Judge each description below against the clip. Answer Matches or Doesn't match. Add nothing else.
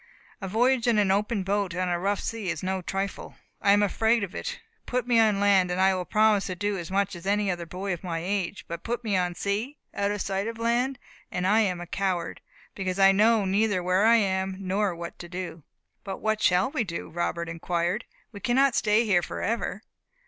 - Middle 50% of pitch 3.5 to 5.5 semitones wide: Doesn't match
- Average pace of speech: Doesn't match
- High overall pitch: Matches